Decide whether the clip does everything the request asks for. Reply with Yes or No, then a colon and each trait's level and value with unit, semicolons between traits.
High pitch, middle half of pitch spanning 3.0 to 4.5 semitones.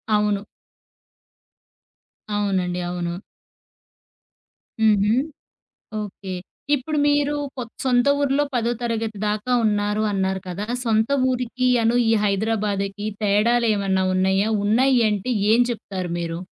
Yes: high, 210 Hz; average, 3.4 semitones